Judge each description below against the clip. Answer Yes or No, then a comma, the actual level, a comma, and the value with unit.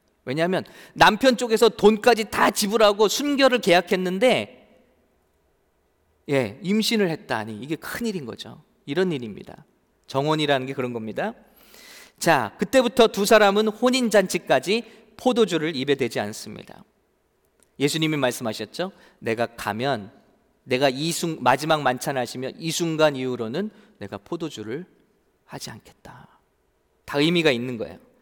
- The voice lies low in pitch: No, medium, 165 Hz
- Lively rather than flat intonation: Yes, wide, 9.0 semitones